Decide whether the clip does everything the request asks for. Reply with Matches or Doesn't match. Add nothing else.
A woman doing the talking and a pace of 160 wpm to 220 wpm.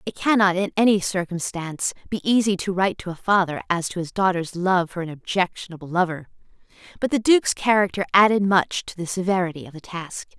Matches